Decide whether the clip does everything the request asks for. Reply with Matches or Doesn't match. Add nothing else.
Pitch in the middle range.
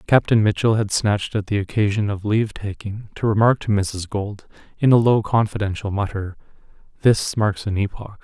Doesn't match